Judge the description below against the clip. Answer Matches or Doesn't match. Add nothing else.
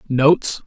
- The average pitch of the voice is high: Doesn't match